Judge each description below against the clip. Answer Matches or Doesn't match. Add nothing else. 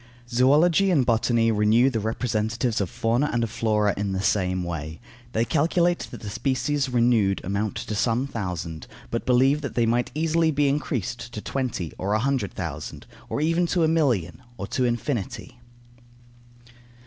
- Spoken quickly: Doesn't match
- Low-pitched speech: Matches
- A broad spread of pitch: Doesn't match